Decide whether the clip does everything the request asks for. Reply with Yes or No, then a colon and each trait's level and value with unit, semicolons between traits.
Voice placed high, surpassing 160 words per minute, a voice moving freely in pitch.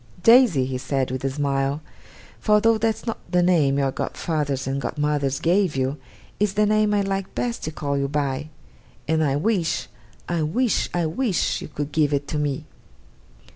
No: medium, 150 Hz; average, 180 wpm; wide, 6.1 semitones